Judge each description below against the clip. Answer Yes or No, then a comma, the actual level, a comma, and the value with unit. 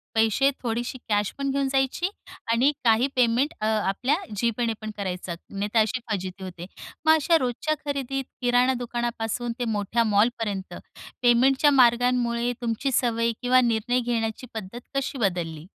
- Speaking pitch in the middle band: No, high, 235 Hz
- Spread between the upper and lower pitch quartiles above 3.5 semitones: No, average, 2.9 semitones